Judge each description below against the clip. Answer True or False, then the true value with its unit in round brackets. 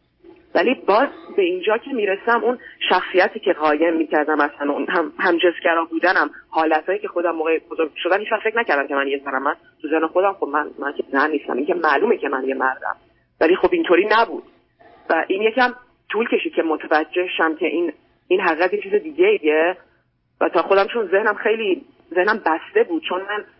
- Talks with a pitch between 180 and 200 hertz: True (185 Hz)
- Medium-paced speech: False (195 wpm)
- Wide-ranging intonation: True (7.6 semitones)